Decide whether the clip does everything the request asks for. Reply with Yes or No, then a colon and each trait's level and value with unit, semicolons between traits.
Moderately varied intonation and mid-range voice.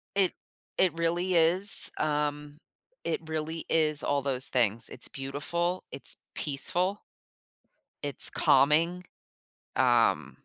Yes: average, 3.4 semitones; medium, 155 Hz